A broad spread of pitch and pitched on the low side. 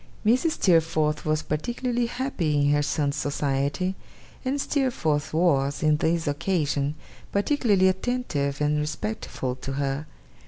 No: wide, 5.8 semitones; medium, 155 Hz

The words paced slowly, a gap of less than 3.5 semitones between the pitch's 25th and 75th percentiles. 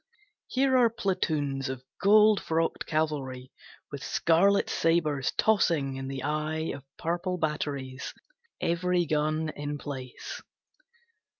No: slow, 110 wpm; average, 4.0 semitones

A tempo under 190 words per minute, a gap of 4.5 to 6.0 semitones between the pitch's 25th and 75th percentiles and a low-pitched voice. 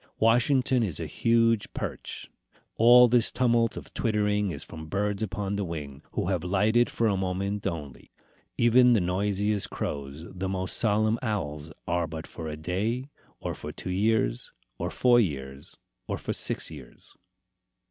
Yes: average, 160 wpm; average, 5.2 semitones; low, 100 Hz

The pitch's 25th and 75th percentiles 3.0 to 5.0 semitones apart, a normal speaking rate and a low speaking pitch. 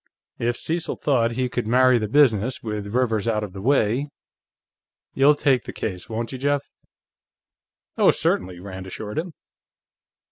Yes: average, 4.1 semitones; average, 150 wpm; low, 115 Hz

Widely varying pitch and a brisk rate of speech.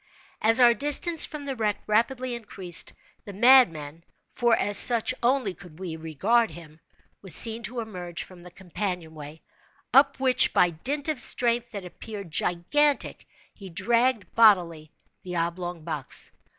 No: wide, 5.8 semitones; average, 145 wpm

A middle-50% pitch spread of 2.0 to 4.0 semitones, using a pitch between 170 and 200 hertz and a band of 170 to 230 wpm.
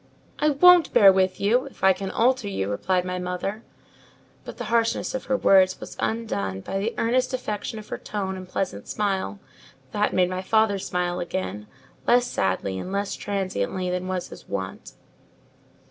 Yes: average, 3.6 semitones; high, 190 Hz; average, 175 wpm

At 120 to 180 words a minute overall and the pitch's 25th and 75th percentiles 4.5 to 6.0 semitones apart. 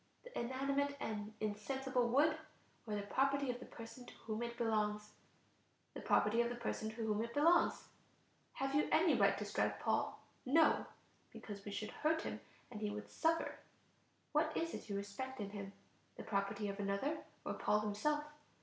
Yes: average, 175 wpm; average, 4.9 semitones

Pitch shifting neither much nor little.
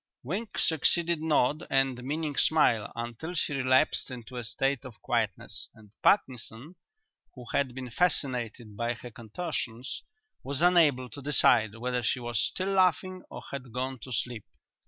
Yes: average, 4.4 semitones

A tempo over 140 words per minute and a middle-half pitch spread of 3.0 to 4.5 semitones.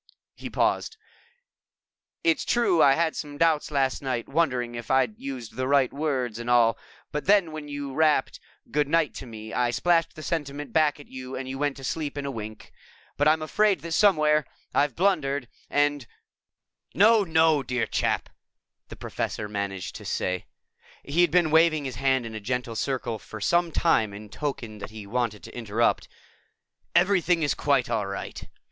No: average, 180 wpm; average, 4.9 semitones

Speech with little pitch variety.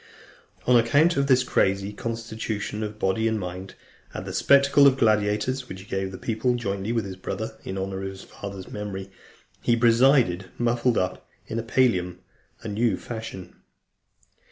No: average, 3.7 semitones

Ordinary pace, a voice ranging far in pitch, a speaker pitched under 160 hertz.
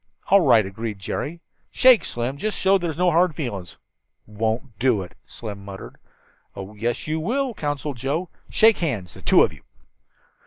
Yes: average, 170 wpm; wide, 8.4 semitones; low, 135 Hz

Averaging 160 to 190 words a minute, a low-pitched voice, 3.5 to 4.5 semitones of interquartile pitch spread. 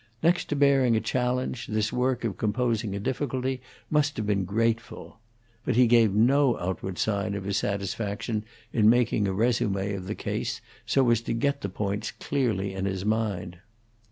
Yes: average, 175 wpm; low, 110 Hz; average, 3.8 semitones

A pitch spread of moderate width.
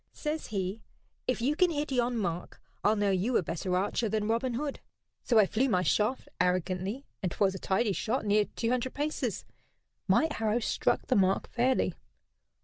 Yes: average, 4.8 semitones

